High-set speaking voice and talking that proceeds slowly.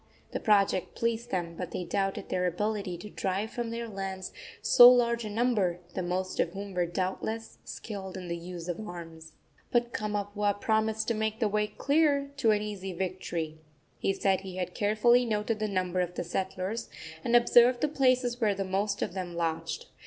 No: high, 200 Hz; average, 190 wpm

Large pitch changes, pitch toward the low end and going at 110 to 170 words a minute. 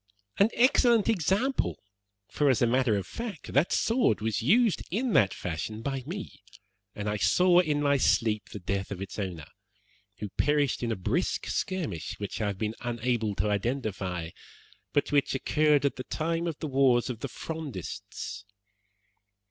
Yes: wide, 7.6 semitones; low, 130 Hz; average, 165 wpm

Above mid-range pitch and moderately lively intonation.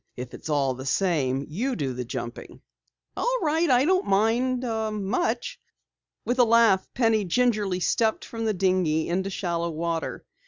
No: high, 195 Hz; wide, 7.2 semitones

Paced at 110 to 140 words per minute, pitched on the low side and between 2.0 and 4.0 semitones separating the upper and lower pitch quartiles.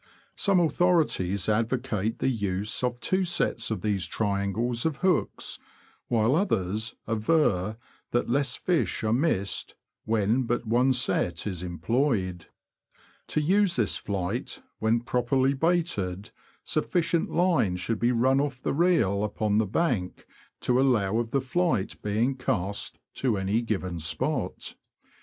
No: slow, 135 wpm; low, 115 Hz; average, 5.3 semitones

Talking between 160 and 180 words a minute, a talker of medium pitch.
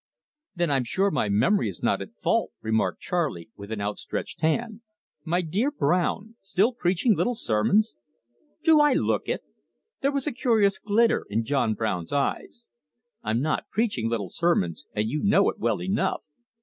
Yes: average, 165 wpm; medium, 175 Hz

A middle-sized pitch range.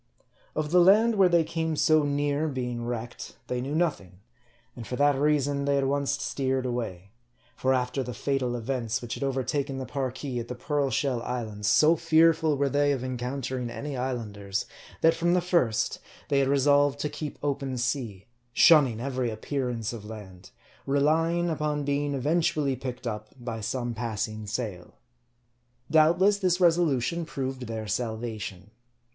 Yes: average, 3.8 semitones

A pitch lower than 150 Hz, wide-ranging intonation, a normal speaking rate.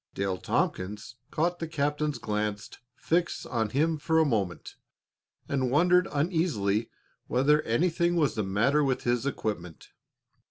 No: medium, 140 Hz; wide, 7.1 semitones; slow, 130 wpm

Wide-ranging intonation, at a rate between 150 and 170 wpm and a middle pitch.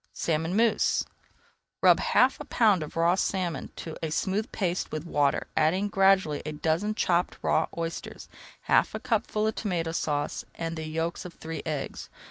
No: average, 3.5 semitones; average, 165 wpm; medium, 170 Hz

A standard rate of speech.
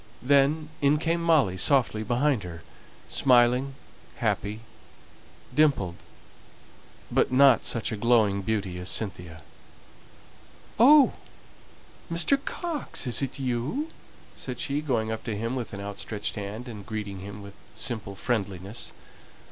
No: slow, 125 wpm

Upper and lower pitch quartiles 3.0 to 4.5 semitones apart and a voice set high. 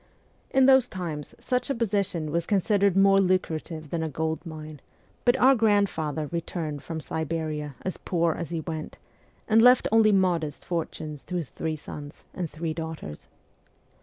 No: average, 4.2 semitones; medium, 170 Hz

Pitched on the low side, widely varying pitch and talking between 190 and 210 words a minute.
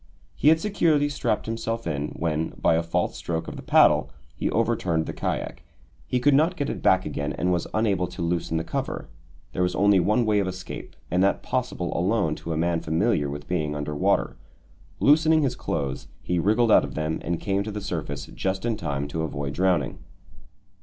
Yes: very low, 90 Hz; wide, 5.9 semitones; average, 200 wpm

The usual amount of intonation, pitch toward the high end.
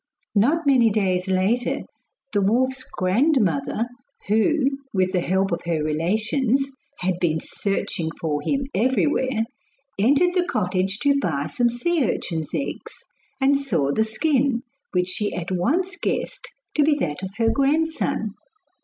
No: wide, 7.0 semitones; high, 220 Hz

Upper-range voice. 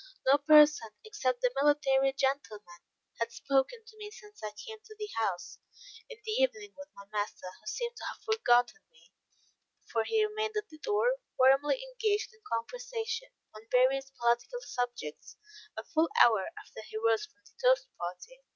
Yes: very high, 295 Hz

